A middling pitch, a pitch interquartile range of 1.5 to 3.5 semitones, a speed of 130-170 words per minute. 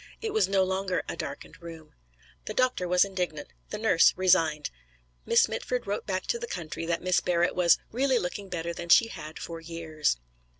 No: medium, 180 Hz; average, 3.0 semitones; average, 185 wpm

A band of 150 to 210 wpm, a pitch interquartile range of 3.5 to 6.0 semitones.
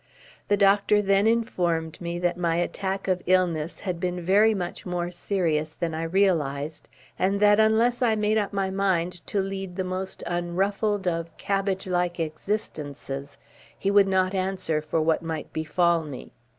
No: average, 165 wpm; average, 2.9 semitones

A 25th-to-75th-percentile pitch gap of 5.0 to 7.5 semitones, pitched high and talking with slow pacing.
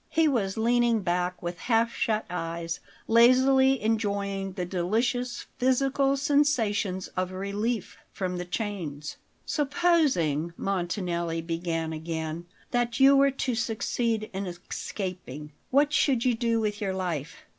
Yes: wide, 5.6 semitones; high, 205 Hz; slow, 125 wpm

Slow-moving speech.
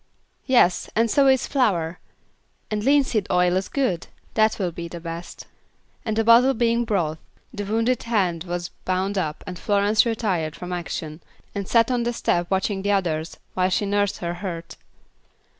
No: average, 170 wpm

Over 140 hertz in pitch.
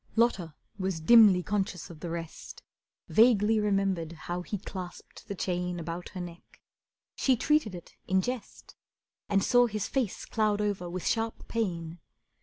Yes: high, 190 Hz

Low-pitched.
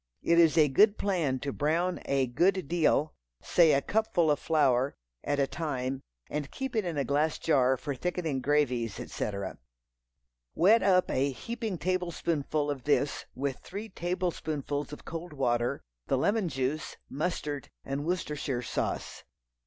No: medium, 150 Hz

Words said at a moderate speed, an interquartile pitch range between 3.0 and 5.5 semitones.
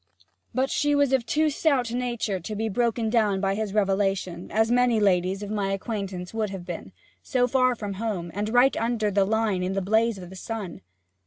No: fast, 210 wpm; average, 3.6 semitones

